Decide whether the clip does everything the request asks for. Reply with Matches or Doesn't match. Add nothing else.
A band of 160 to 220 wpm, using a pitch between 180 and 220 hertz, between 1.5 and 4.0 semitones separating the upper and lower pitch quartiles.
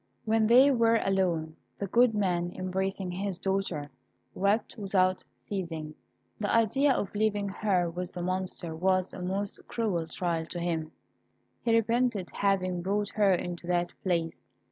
Doesn't match